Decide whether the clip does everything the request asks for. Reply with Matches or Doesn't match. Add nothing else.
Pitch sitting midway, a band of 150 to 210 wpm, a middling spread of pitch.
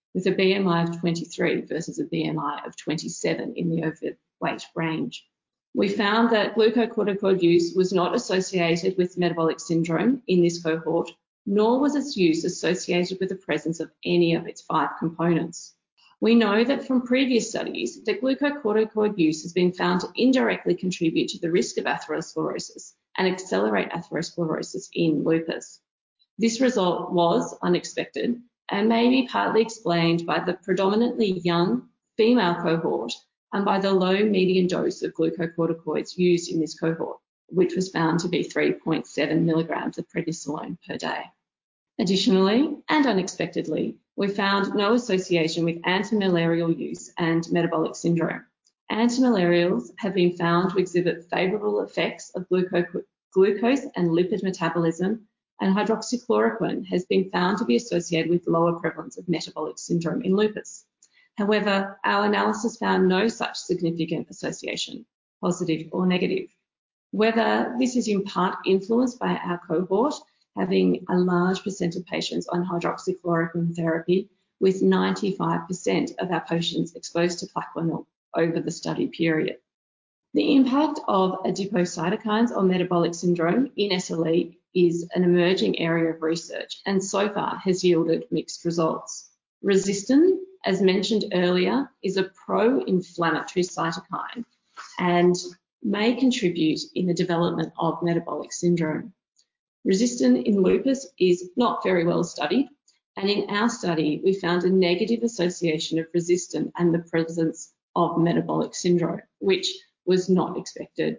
Doesn't match